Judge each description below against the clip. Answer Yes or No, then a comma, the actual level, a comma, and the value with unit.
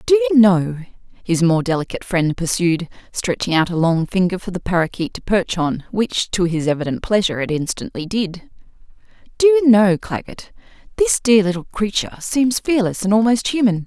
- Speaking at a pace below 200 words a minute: Yes, average, 175 wpm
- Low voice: No, high, 195 Hz